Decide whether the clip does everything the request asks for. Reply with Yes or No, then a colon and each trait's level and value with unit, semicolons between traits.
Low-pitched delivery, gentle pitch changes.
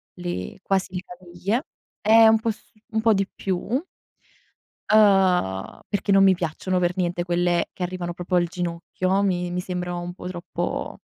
No: medium, 180 Hz; narrow, 2.0 semitones